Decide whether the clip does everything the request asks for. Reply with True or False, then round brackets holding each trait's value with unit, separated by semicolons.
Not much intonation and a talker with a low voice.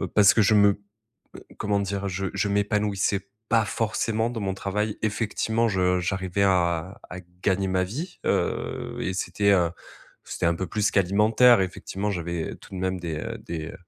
True (2.3 semitones; 100 Hz)